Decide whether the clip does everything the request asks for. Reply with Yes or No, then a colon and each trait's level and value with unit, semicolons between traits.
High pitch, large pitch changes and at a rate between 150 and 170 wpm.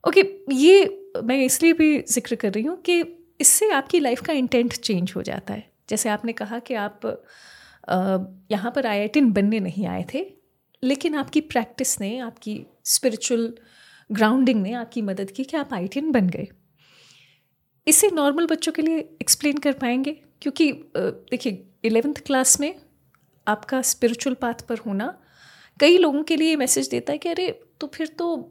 Yes: very high, 260 Hz; wide, 5.7 semitones; average, 165 wpm